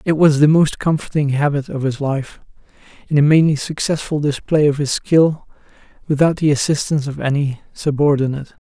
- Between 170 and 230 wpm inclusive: No, average, 160 wpm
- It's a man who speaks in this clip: Yes, male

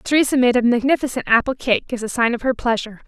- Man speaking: No, female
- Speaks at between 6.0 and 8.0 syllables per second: Yes, 6.7 syllables/s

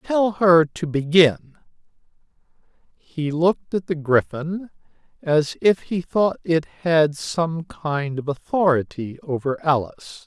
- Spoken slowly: Yes, slow, 125 wpm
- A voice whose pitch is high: No, medium, 160 Hz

